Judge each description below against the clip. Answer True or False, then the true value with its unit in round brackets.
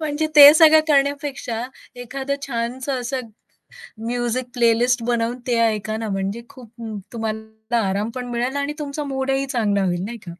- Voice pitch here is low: False (245 Hz)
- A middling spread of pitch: True (3.5 semitones)